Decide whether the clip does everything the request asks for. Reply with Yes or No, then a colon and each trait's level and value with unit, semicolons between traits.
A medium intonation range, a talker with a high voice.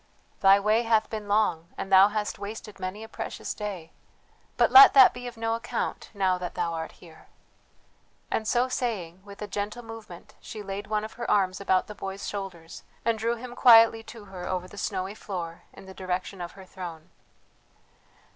Yes: average, 3.2 semitones; high, 200 Hz